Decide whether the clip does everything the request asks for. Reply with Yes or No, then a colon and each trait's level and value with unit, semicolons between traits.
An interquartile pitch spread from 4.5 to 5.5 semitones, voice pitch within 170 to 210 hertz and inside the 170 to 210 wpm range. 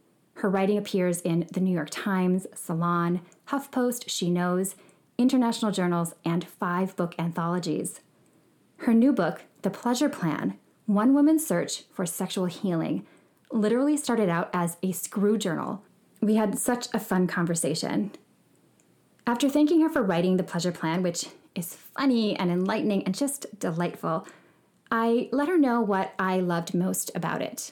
No: average, 5.1 semitones; high, 190 Hz; average, 150 wpm